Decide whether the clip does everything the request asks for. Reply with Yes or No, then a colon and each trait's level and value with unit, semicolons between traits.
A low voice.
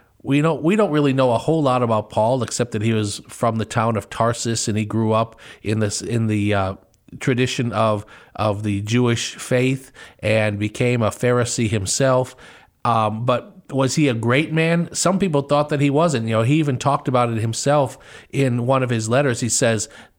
Yes: low, 120 Hz